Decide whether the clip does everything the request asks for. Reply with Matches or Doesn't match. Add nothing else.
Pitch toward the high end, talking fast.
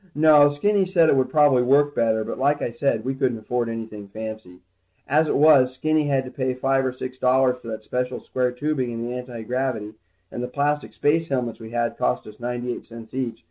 Doesn't match